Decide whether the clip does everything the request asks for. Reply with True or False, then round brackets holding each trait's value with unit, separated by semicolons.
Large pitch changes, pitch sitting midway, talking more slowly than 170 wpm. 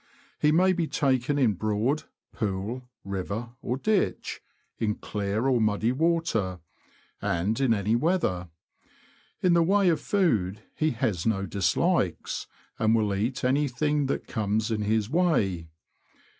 False (6.4 semitones; 115 Hz; 135 wpm)